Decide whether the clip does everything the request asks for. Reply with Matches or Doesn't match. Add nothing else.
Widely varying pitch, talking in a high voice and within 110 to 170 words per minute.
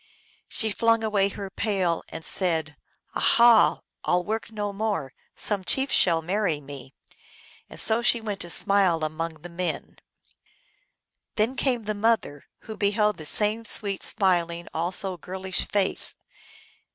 Doesn't match